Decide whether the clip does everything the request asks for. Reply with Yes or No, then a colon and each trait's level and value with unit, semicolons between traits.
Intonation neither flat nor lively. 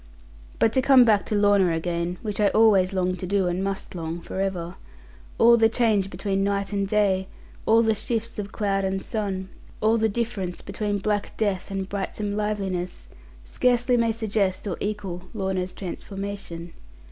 No: narrow, 2.3 semitones